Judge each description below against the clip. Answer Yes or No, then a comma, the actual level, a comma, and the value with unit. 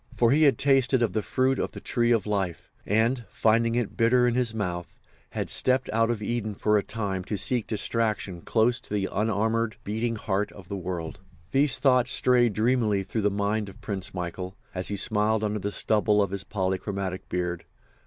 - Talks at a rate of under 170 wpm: No, average, 195 wpm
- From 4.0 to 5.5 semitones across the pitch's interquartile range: No, average, 3.2 semitones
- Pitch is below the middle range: Yes, low, 110 Hz